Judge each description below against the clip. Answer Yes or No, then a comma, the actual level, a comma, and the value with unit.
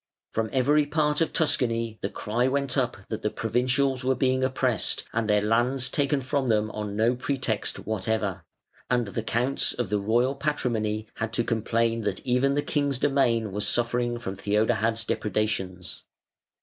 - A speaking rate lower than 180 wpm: Yes, average, 160 wpm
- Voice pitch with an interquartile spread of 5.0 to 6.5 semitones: No, average, 3.4 semitones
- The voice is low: Yes, low, 120 Hz